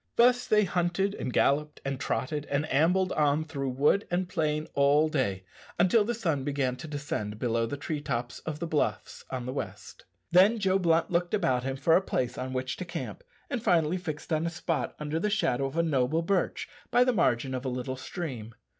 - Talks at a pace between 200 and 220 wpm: Yes, fast, 205 wpm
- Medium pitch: Yes, medium, 150 Hz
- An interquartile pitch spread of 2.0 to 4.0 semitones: No, average, 5.2 semitones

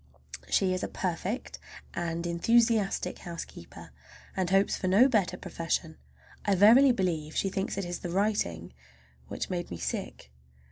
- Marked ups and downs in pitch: No, average, 3.2 semitones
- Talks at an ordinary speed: Yes, average, 145 wpm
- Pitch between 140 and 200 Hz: Yes, medium, 185 Hz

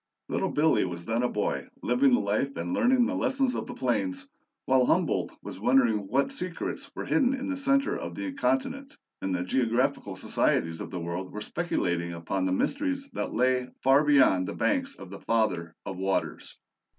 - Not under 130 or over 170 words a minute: No, average, 185 wpm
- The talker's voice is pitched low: Yes, low, 130 Hz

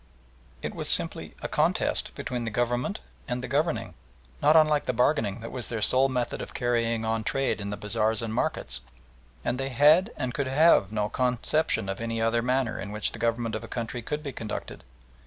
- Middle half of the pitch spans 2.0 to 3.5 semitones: Yes, average, 3.0 semitones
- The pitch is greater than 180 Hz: No, low, 120 Hz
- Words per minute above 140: Yes, average, 200 wpm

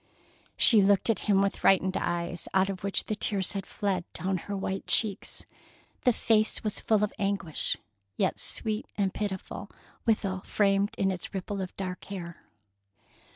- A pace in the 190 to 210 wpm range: No, average, 160 wpm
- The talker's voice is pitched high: Yes, high, 195 Hz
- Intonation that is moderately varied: No, narrow, 1.6 semitones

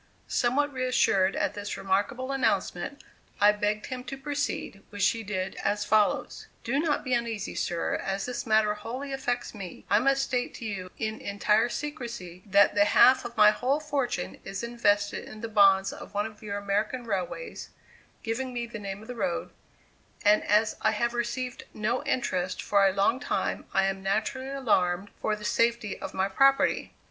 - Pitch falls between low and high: No, high, 220 Hz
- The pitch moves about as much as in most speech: Yes, average, 3.7 semitones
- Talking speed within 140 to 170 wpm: No, average, 180 wpm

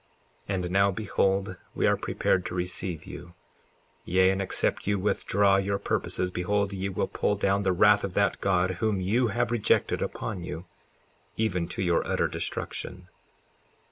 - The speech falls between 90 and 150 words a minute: No, average, 165 wpm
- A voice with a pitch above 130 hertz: No, very low, 95 Hz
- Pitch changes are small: Yes, narrow, 1.9 semitones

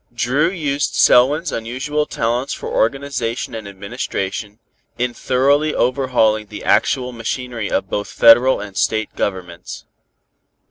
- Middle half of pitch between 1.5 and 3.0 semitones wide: No, average, 4.0 semitones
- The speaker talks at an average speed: No, slow, 120 wpm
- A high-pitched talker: No, low, 120 Hz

